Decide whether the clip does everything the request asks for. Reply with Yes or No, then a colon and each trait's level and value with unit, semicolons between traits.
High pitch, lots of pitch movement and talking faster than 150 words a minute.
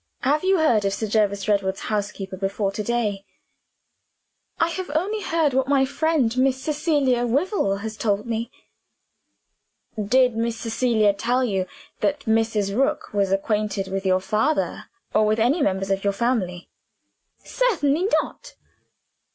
No: high, 225 Hz; wide, 5.8 semitones; average, 145 wpm